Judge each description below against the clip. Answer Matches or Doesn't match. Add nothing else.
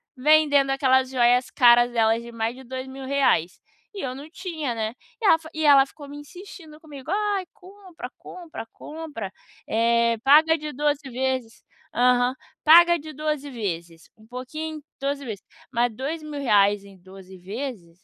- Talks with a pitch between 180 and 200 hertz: Doesn't match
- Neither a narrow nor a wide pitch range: Matches